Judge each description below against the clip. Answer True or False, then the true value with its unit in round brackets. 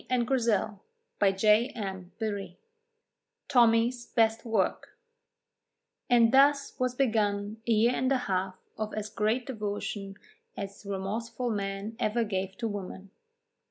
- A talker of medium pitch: False (215 Hz)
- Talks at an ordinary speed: False (110 wpm)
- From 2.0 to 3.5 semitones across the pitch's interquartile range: True (3.1 semitones)